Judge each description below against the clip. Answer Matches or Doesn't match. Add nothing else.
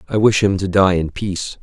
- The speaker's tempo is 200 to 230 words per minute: Doesn't match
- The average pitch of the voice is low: Matches